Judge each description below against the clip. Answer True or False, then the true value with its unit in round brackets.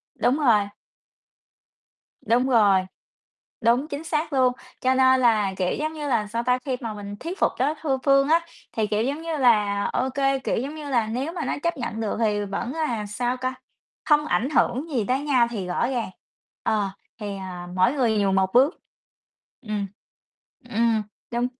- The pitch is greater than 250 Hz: False (245 Hz)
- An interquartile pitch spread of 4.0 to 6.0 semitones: True (4.5 semitones)